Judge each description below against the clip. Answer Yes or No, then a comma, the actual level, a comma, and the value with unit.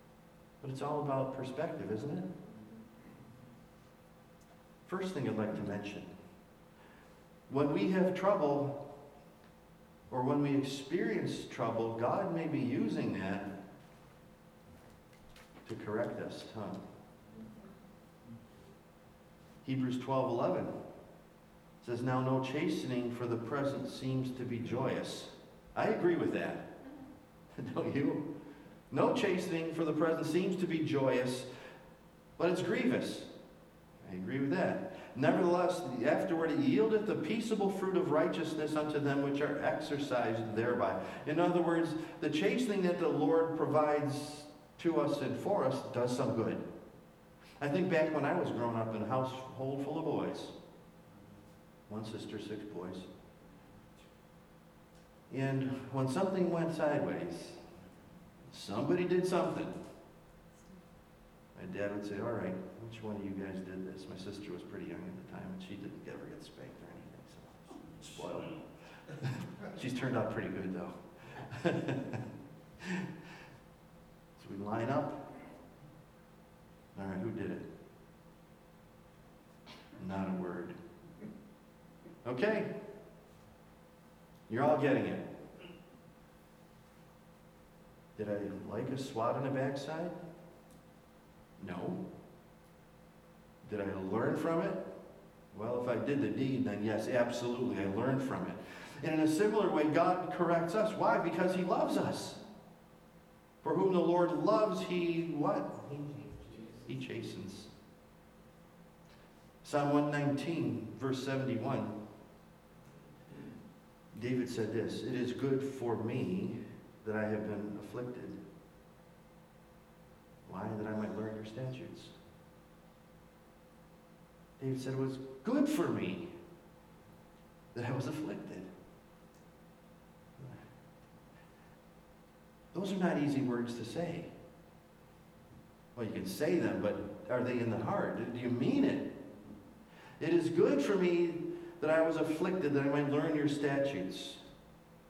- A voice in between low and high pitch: Yes, medium, 145 Hz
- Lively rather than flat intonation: Yes, wide, 6.1 semitones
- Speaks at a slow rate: Yes, slow, 125 wpm